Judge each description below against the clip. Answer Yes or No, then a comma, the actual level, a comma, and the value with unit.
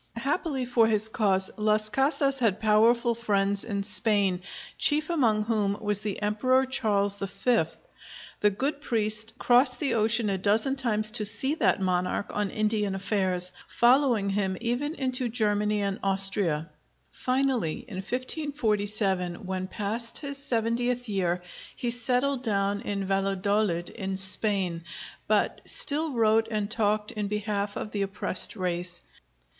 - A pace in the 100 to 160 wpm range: Yes, average, 140 wpm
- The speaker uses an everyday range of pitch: Yes, average, 3.6 semitones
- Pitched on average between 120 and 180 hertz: No, high, 215 Hz